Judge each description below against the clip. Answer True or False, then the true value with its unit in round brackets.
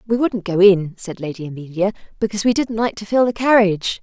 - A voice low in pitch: False (200 Hz)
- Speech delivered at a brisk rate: True (225 wpm)